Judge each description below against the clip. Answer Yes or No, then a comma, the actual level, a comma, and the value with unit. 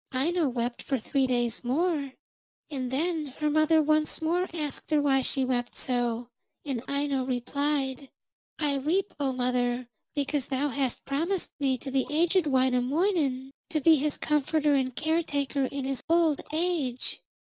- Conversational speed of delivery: Yes, average, 150 wpm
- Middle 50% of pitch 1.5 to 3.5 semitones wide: Yes, average, 3.2 semitones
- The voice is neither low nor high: No, very high, 280 Hz